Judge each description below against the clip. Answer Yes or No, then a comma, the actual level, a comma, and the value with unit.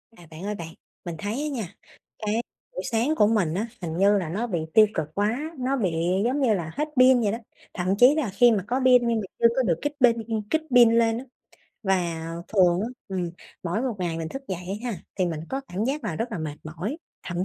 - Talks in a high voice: Yes, high, 210 Hz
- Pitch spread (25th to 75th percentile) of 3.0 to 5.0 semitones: No, wide, 5.5 semitones